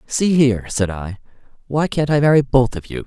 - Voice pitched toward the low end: Yes, low, 130 Hz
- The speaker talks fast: Yes, fast, 215 wpm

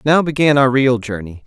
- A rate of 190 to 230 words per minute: Yes, fast, 205 wpm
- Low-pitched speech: Yes, low, 130 Hz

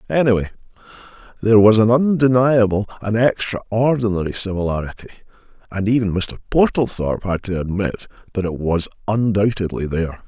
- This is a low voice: Yes, low, 105 Hz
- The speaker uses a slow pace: Yes, slow, 105 wpm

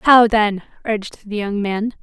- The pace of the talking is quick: No, average, 180 wpm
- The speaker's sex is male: No, female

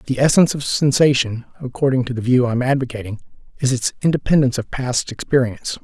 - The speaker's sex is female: No, male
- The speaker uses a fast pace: No, average, 175 wpm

